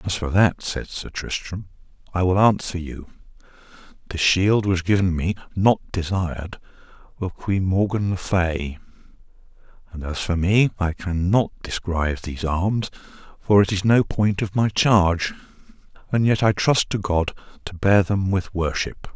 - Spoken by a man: Yes, male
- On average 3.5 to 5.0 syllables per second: Yes, 4.5 syllables/s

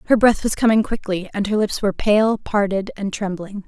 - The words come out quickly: Yes, fast, 210 wpm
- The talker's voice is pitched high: Yes, high, 205 Hz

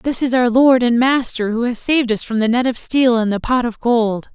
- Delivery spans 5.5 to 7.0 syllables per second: No, 5.1 syllables/s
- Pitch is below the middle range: No, high, 240 Hz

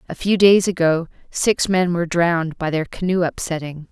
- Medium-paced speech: Yes, average, 185 wpm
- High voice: No, medium, 170 Hz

